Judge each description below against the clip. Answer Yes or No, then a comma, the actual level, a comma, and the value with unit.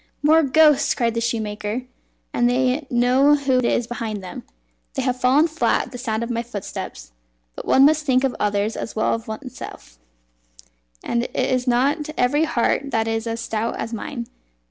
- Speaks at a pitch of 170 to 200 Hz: No, high, 245 Hz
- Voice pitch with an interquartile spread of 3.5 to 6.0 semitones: No, average, 3.1 semitones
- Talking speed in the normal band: Yes, average, 180 wpm